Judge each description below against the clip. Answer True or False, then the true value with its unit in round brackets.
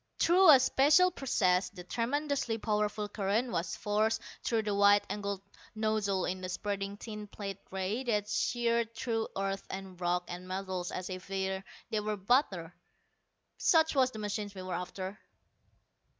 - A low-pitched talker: False (205 Hz)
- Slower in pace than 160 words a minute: True (150 wpm)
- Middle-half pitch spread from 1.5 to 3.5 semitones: True (3.2 semitones)